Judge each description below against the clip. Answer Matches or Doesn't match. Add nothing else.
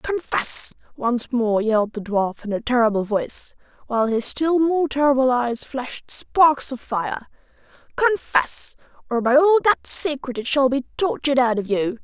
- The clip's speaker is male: Doesn't match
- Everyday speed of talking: Matches